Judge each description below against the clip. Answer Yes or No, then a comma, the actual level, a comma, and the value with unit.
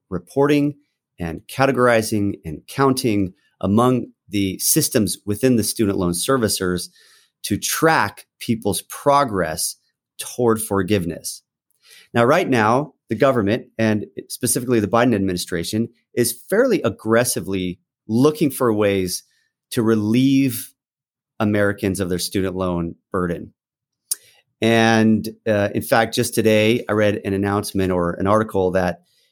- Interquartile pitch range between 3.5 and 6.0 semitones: Yes, average, 4.3 semitones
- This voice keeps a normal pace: No, slow, 115 wpm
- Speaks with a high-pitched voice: No, low, 110 Hz